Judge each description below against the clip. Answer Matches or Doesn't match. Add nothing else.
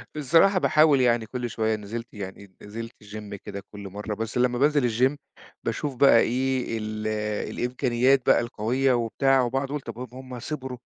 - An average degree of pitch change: Matches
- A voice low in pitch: Matches